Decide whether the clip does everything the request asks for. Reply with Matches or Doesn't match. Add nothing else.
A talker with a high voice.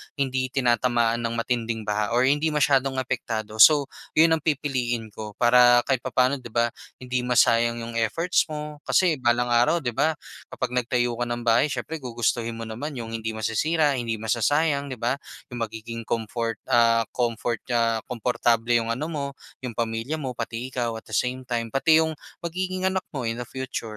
Doesn't match